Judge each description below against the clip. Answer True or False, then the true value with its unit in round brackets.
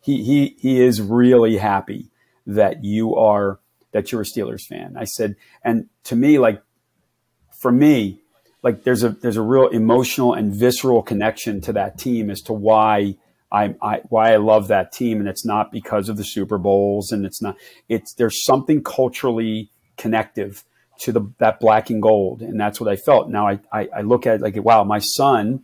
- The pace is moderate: True (195 wpm)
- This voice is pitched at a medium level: False (110 Hz)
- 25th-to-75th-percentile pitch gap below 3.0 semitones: True (2.6 semitones)